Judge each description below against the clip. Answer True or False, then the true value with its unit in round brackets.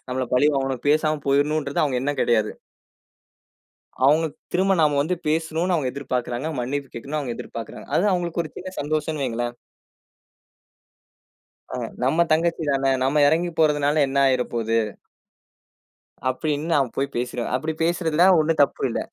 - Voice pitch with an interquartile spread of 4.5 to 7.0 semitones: False (3.6 semitones)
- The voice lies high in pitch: False (145 Hz)